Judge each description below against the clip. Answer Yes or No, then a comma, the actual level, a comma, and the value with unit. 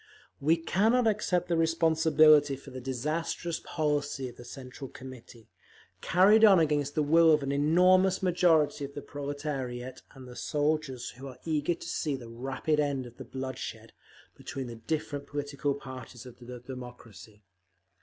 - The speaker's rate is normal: Yes, average, 155 wpm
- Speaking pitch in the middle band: Yes, medium, 145 Hz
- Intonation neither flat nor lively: Yes, average, 3.8 semitones